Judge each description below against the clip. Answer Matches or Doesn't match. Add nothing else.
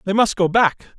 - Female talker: Doesn't match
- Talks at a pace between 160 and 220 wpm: Doesn't match